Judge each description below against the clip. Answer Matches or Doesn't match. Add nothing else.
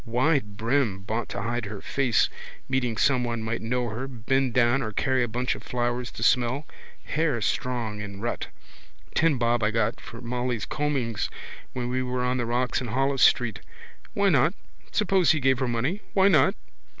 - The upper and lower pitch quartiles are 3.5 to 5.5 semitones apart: Doesn't match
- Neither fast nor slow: Matches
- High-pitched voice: Doesn't match